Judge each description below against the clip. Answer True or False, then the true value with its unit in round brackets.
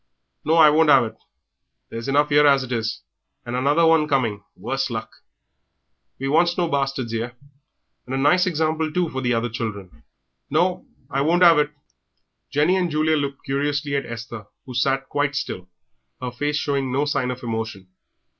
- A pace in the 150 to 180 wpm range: True (175 wpm)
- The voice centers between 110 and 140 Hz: True (135 Hz)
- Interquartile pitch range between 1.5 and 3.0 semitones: False (3.7 semitones)